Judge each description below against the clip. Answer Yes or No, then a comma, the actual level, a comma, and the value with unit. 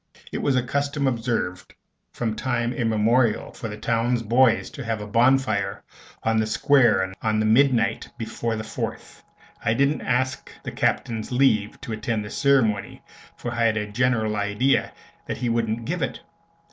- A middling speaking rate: Yes, average, 165 wpm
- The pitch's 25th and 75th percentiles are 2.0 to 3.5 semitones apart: Yes, average, 2.8 semitones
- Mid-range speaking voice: No, low, 115 Hz